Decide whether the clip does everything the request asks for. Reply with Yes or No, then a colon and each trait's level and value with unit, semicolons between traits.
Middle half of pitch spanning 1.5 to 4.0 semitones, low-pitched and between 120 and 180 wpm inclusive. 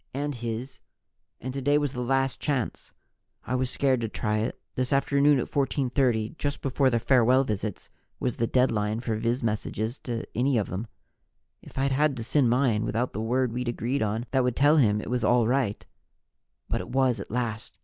No: average, 2.9 semitones; low, 125 Hz; average, 195 wpm